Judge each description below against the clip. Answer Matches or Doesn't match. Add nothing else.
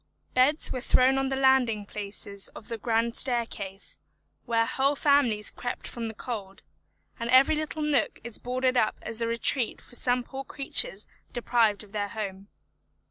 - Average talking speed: Matches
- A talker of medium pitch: Doesn't match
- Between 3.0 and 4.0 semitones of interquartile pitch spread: Matches